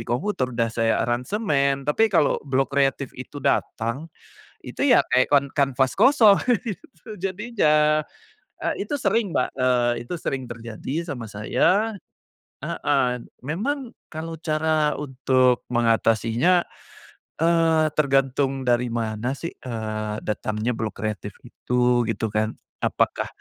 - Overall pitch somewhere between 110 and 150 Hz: Yes, low, 135 Hz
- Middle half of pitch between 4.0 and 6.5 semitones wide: Yes, average, 5.2 semitones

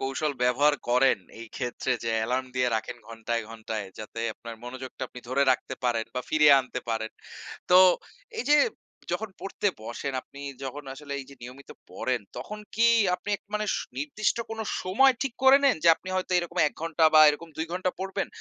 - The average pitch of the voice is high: No, medium, 140 Hz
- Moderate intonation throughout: No, wide, 6.8 semitones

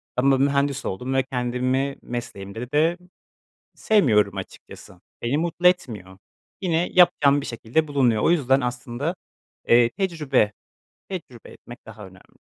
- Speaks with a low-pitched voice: Yes, low, 130 Hz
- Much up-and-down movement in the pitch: No, average, 4.6 semitones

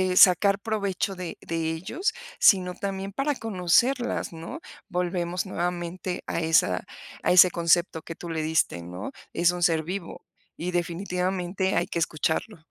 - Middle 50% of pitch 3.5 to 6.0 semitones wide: No, narrow, 2.5 semitones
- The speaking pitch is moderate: Yes, medium, 180 Hz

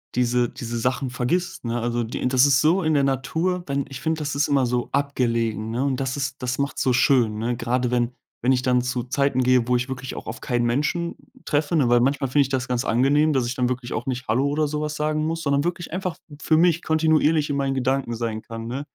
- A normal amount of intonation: Yes, average, 3.1 semitones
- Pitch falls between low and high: No, low, 130 Hz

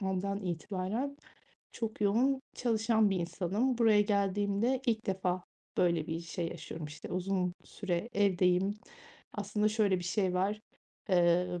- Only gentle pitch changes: No, average, 3.0 semitones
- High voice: Yes, high, 195 Hz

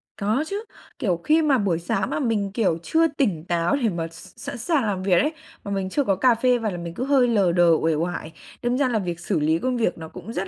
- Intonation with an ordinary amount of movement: No, wide, 6.5 semitones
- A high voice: Yes, high, 200 Hz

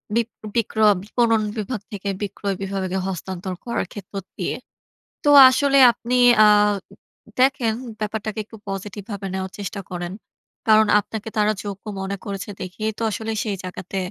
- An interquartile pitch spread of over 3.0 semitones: No, narrow, 2.4 semitones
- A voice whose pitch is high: Yes, high, 205 Hz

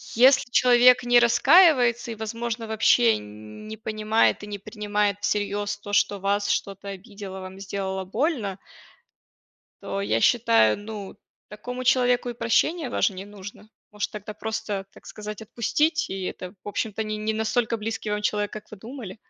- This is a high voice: Yes, high, 215 Hz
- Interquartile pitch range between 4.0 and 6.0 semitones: No, average, 2.8 semitones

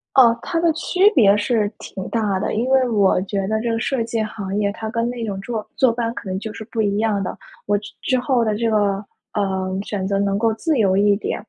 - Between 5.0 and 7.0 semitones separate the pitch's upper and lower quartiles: No, average, 2.7 semitones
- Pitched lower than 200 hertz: No, high, 220 Hz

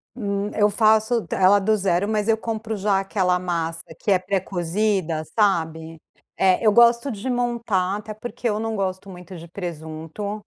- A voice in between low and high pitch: No, high, 200 Hz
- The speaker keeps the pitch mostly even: No, average, 3.2 semitones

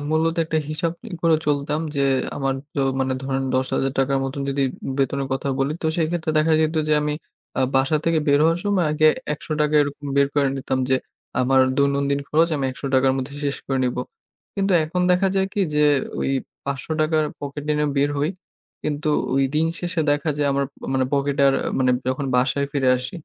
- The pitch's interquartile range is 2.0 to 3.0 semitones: Yes, narrow, 2.5 semitones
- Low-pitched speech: No, medium, 145 Hz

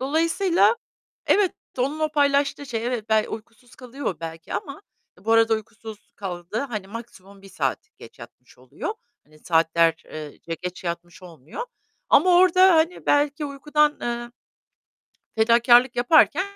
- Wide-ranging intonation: Yes, wide, 7.1 semitones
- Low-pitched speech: No, high, 235 Hz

